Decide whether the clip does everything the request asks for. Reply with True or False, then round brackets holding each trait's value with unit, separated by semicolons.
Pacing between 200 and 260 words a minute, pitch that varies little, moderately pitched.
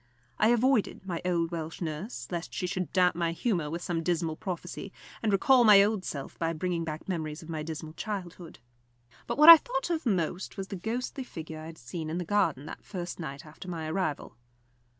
False (205 wpm; 3.8 semitones; 175 Hz)